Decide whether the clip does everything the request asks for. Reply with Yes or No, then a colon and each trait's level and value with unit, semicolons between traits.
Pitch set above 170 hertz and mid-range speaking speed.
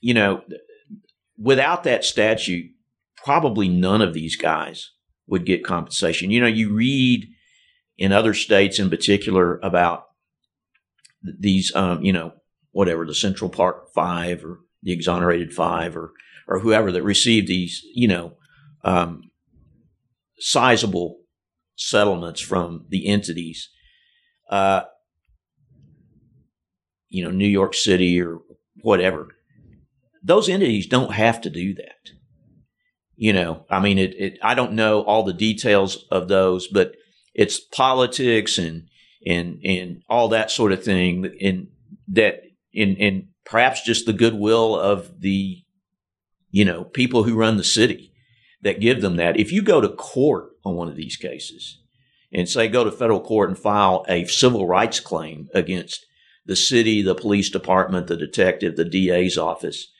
No: low, 100 Hz; average, 145 wpm